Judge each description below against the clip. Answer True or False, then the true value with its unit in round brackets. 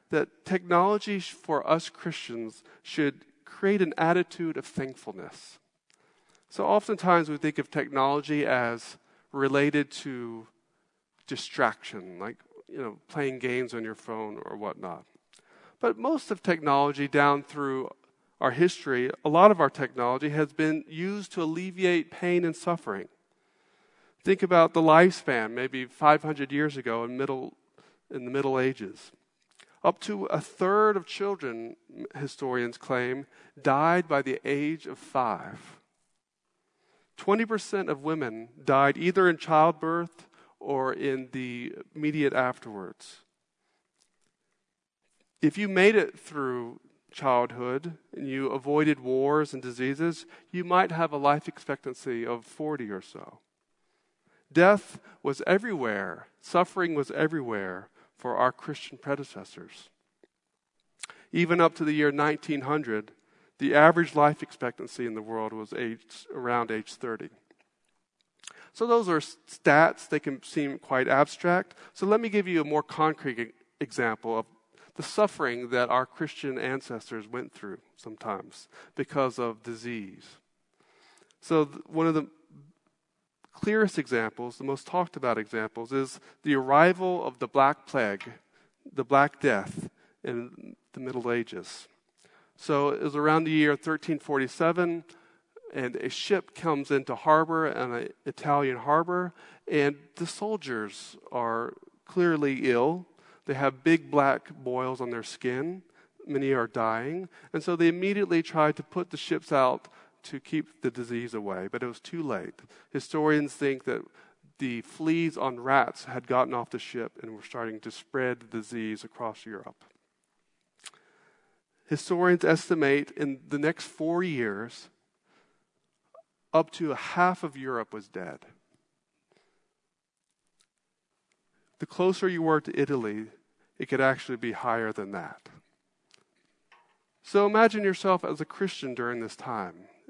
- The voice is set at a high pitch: False (150 Hz)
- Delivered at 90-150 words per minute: True (135 wpm)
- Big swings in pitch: False (4.9 semitones)